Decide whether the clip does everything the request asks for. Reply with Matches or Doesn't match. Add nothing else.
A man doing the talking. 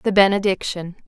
Doesn't match